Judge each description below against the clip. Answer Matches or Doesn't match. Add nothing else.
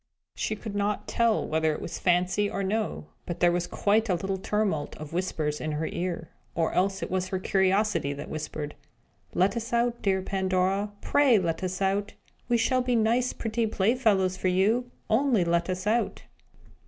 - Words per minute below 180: Doesn't match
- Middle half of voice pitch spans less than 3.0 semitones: Doesn't match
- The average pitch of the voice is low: Doesn't match